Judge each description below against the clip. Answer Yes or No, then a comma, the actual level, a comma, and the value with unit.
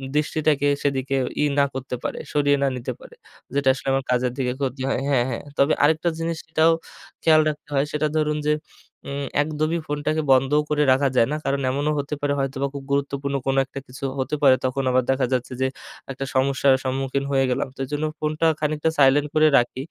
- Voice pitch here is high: No, medium, 140 Hz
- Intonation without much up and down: Yes, narrow, 2.1 semitones